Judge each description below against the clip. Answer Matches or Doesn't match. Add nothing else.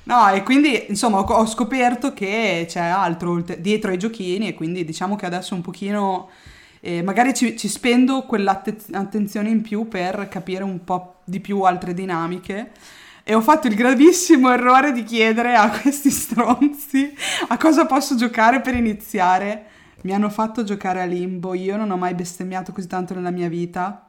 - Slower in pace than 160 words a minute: Doesn't match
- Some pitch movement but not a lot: Matches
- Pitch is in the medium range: Doesn't match